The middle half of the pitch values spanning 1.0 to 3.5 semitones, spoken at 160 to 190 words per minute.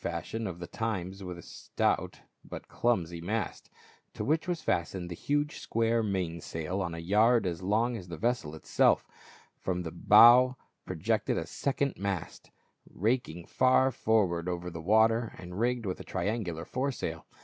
No: average, 5.2 semitones; average, 170 wpm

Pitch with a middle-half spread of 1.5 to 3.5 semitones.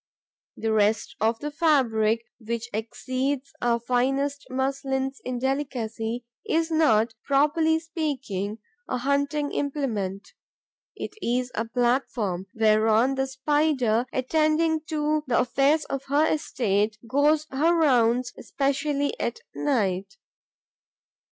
No: average, 4.3 semitones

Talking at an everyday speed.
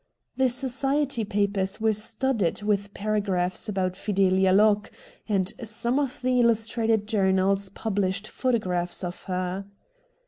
No: slow, 125 wpm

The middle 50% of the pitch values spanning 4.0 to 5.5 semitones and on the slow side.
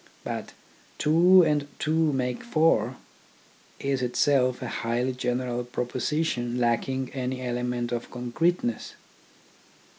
No: average, 3.3 semitones; slow, 120 wpm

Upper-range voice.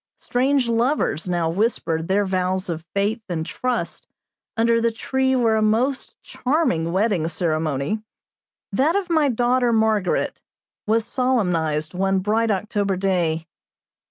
Yes: high, 210 Hz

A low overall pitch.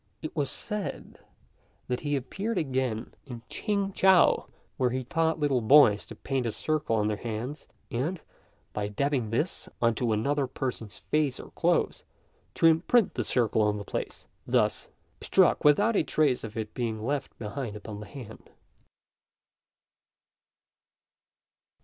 Yes: low, 130 Hz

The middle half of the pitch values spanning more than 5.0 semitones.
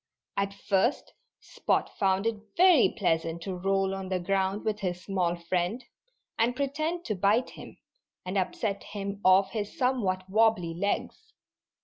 No: average, 3.2 semitones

